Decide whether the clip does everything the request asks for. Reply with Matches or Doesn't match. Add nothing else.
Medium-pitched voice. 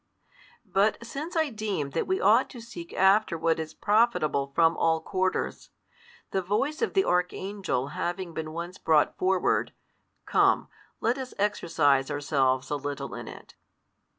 Matches